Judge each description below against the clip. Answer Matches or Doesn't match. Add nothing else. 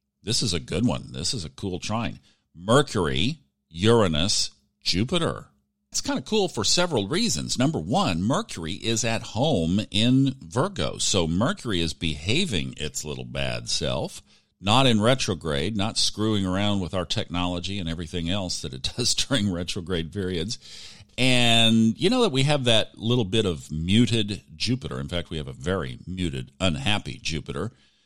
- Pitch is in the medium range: Doesn't match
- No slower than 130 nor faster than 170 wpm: Matches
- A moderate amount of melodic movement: Doesn't match